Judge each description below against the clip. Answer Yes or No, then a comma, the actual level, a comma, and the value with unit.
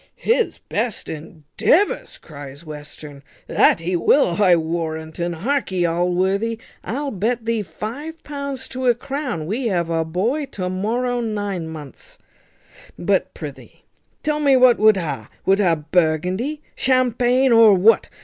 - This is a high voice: Yes, high, 205 Hz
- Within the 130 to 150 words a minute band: Yes, average, 140 wpm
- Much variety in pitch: Yes, wide, 7.2 semitones